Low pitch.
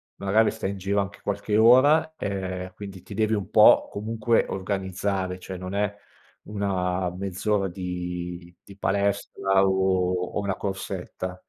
Yes: very low, 95 Hz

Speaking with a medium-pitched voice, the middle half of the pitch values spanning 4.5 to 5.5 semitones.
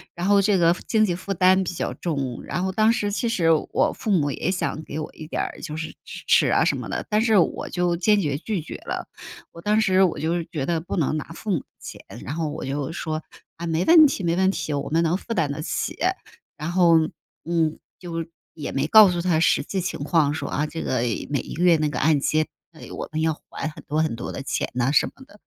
No: medium, 170 Hz; average, 3.5 semitones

